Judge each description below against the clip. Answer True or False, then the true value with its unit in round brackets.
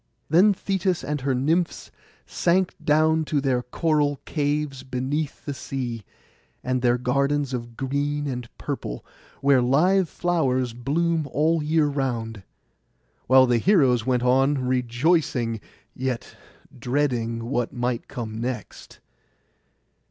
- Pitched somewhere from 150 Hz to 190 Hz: False (135 Hz)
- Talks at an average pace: False (120 wpm)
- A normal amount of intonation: True (3.5 semitones)